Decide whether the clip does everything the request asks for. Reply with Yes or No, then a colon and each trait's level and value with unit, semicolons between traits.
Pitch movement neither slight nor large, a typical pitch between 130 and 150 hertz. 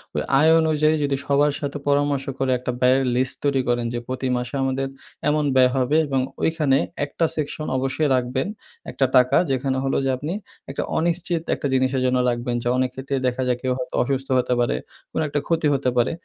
No: narrow, 2.3 semitones; low, 135 Hz